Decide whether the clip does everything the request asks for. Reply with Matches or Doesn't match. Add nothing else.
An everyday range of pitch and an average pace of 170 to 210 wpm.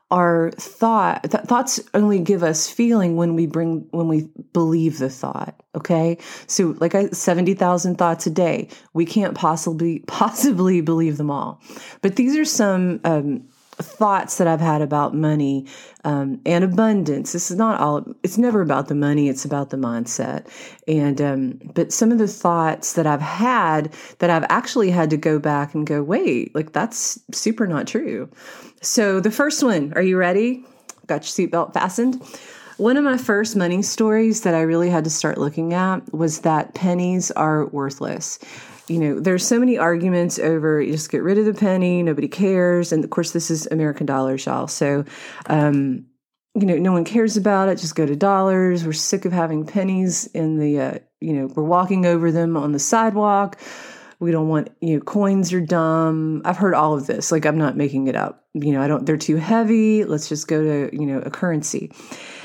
Matches